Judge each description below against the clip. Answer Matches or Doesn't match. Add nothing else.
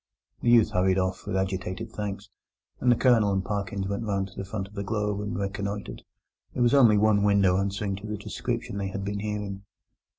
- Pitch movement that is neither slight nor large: Doesn't match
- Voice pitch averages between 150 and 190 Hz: Doesn't match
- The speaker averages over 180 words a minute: Matches